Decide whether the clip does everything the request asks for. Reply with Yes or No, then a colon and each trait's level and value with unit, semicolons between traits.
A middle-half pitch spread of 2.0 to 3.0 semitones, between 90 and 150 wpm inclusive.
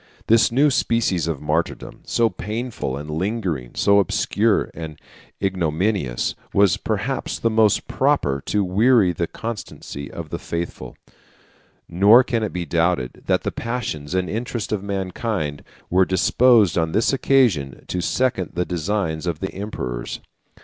No: wide, 5.4 semitones; average, 140 wpm